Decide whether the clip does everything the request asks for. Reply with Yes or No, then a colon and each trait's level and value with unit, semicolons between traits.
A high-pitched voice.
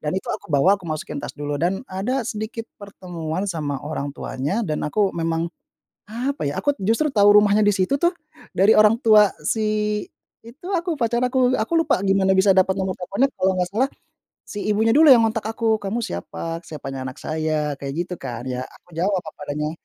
Yes: high, 195 Hz